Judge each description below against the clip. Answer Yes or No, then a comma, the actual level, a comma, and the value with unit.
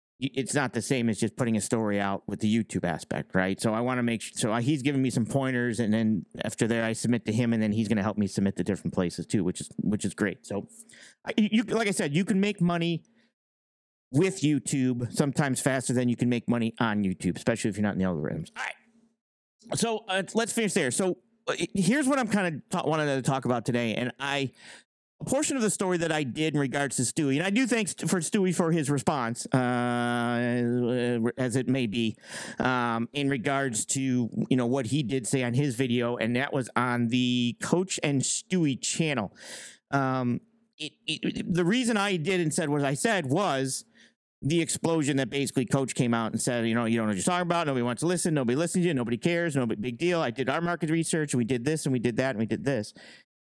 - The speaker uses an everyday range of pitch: No, wide, 6.1 semitones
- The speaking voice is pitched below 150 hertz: Yes, low, 135 Hz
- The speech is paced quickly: Yes, fast, 235 wpm